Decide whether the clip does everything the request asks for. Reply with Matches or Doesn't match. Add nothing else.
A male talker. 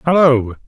Matches